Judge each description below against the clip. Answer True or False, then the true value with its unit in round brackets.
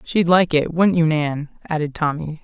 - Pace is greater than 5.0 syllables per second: False (4.7 syllables/s)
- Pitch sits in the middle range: True (160 Hz)